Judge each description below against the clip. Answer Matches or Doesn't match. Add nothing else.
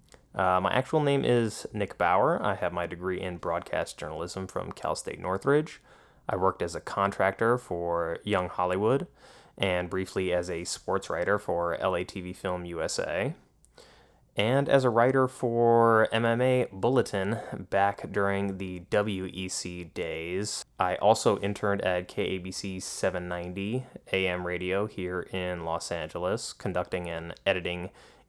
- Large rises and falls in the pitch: Doesn't match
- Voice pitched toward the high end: Doesn't match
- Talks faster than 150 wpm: Doesn't match